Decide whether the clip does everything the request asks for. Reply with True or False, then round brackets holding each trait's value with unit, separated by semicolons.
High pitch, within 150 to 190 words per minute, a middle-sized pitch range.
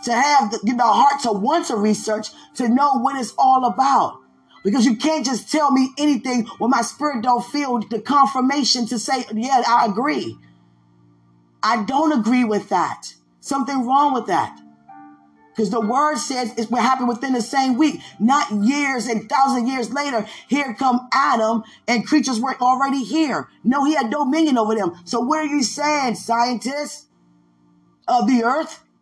True (245 Hz; 175 wpm; 4.0 semitones)